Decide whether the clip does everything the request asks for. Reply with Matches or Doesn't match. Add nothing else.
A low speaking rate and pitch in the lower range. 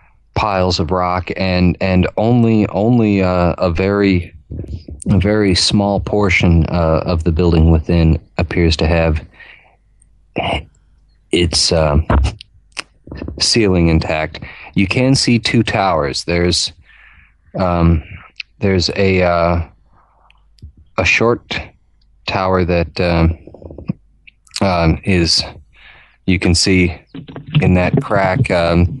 Matches